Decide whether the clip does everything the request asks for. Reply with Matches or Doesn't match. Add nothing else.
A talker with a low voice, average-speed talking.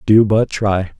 Matches